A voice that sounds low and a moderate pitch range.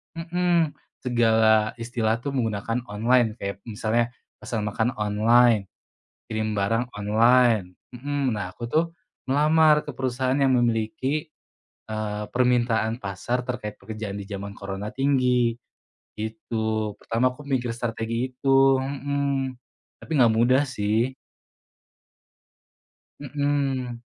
Yes: low, 120 Hz; average, 3.4 semitones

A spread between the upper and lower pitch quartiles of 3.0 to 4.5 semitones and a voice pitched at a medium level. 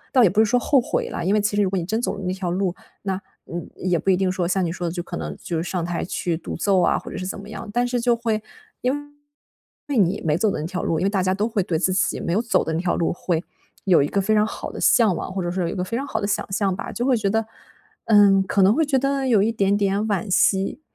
No: average, 3.3 semitones; high, 195 Hz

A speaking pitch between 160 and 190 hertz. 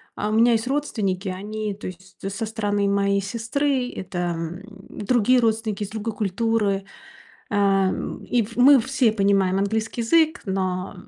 No: high, 210 Hz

